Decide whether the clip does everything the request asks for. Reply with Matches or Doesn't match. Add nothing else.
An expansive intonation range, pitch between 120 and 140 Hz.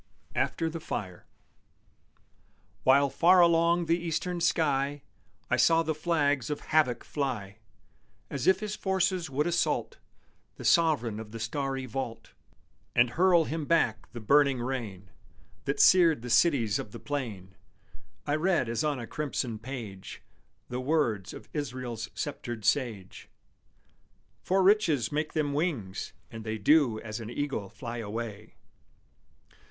Matches